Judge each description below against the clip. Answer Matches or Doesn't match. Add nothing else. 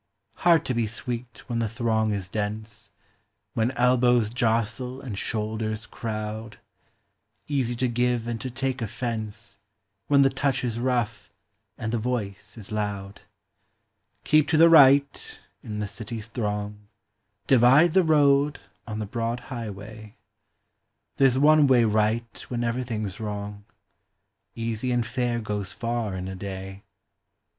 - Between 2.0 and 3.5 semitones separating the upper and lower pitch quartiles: Matches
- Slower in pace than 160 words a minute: Matches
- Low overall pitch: Matches